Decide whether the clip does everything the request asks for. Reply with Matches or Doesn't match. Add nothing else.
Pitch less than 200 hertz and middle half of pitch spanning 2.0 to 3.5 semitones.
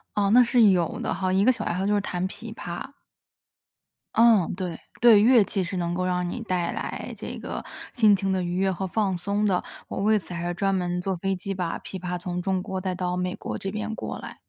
Matches